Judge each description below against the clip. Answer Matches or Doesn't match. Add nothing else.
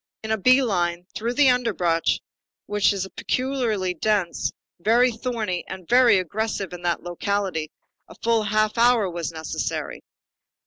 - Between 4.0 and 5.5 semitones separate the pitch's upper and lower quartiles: Matches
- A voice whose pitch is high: Matches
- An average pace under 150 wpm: Matches